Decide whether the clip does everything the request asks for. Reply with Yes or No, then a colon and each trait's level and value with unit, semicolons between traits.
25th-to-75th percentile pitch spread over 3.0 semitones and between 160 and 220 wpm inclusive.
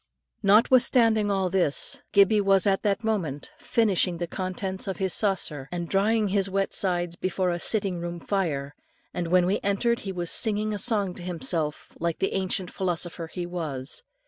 No: average, 2.7 semitones; average, 170 wpm